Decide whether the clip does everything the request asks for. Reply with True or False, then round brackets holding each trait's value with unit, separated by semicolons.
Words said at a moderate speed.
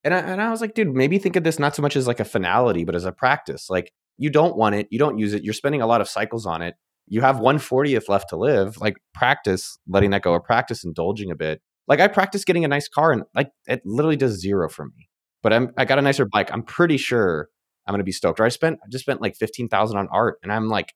False (280 wpm)